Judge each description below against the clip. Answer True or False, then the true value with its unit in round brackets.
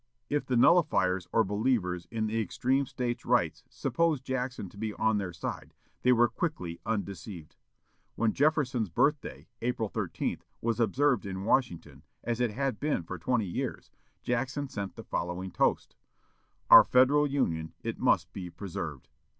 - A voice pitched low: True (115 Hz)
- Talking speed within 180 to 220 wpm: False (150 wpm)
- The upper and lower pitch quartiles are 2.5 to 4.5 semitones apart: False (5.6 semitones)